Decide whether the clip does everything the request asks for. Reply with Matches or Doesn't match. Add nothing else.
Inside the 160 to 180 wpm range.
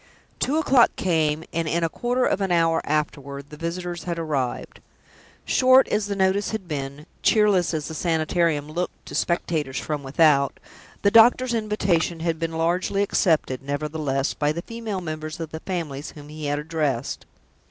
Matches